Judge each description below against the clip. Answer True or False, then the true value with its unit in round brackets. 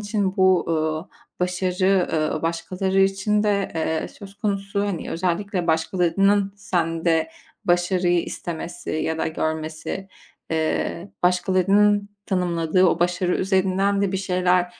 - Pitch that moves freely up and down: False (2.6 semitones)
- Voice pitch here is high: False (180 Hz)